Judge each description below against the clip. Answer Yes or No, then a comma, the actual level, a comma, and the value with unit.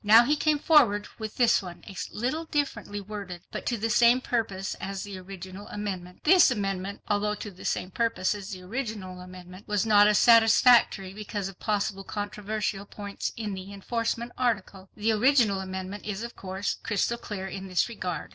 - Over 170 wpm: Yes, average, 180 wpm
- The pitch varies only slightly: No, average, 3.1 semitones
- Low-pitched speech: No, high, 205 Hz